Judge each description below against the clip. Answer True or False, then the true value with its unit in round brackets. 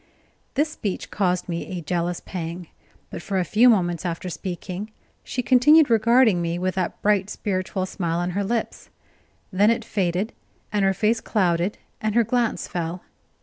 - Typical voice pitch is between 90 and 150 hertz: False (190 Hz)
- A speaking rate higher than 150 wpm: True (165 wpm)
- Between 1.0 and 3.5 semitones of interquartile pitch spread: False (3.9 semitones)